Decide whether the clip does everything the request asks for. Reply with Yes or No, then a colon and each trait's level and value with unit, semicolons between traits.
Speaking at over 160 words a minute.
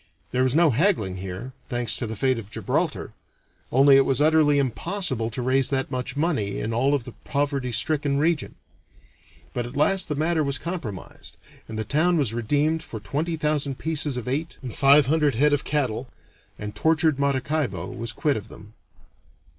Yes: average, 180 wpm